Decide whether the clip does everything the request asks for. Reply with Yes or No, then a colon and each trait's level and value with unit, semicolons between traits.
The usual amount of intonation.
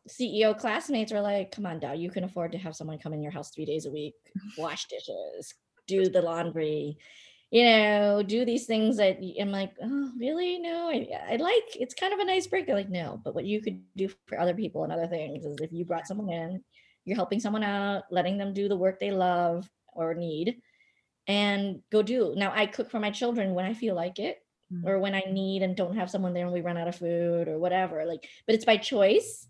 Yes: average, 4.2 semitones